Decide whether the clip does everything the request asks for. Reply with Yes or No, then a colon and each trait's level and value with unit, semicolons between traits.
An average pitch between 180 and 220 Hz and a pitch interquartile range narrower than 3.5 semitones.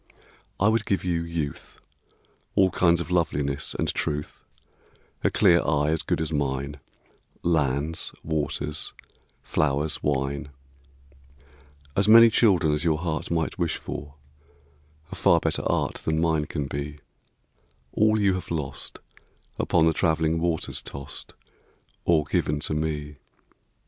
No: very low, 80 Hz; narrow, 2.6 semitones